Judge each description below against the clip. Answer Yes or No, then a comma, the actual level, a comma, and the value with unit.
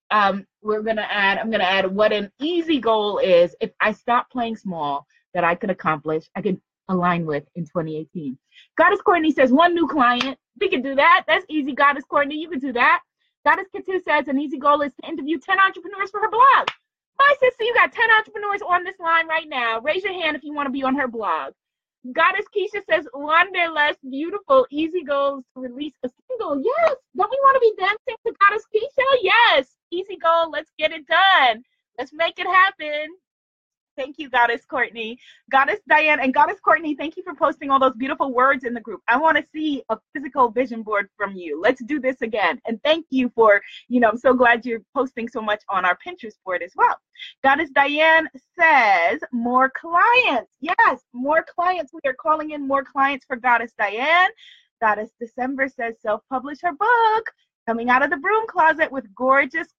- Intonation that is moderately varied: No, wide, 6.3 semitones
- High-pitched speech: Yes, very high, 290 Hz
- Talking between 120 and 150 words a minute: No, fast, 205 wpm